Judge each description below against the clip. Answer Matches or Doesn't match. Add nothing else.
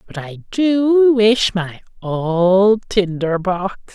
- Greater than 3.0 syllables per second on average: Doesn't match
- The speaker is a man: Matches